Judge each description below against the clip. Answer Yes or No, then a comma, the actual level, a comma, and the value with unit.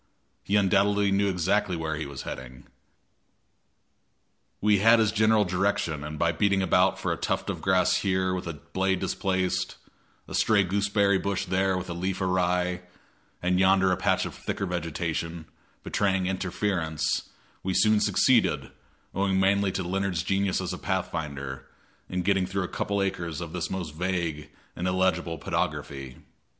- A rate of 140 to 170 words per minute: Yes, average, 160 wpm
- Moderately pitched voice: No, very low, 95 Hz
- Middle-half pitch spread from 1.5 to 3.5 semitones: Yes, narrow, 2.5 semitones